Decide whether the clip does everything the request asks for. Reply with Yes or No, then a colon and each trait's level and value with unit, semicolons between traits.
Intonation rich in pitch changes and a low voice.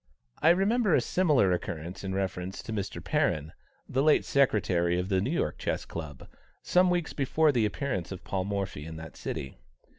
Yes: wide, 8.4 semitones; low, 100 Hz